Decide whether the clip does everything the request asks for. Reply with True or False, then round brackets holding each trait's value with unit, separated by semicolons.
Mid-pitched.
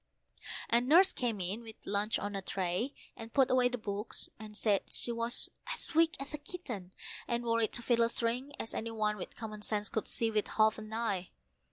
False (225 Hz)